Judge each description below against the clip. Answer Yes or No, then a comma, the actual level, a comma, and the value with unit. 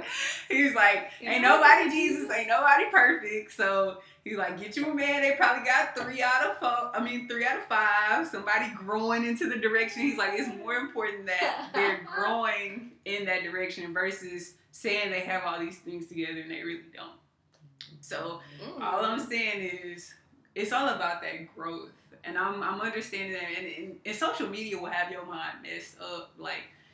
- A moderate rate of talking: Yes, average, 185 wpm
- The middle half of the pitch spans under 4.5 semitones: No, average, 5.0 semitones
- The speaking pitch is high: Yes, high, 205 Hz